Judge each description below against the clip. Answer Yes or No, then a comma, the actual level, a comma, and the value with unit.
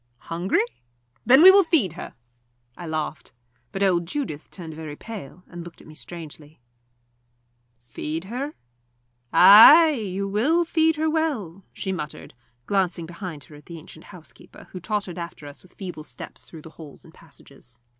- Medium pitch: Yes, medium, 180 Hz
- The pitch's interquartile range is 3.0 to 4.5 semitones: No, wide, 5.6 semitones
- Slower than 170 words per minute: Yes, average, 160 wpm